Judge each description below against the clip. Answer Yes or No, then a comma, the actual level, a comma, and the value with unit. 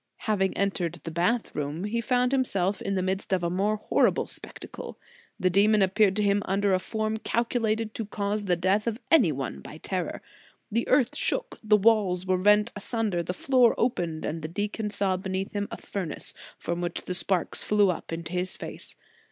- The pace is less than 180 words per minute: No, average, 195 wpm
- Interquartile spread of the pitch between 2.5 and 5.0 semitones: Yes, average, 3.1 semitones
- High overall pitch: Yes, high, 200 Hz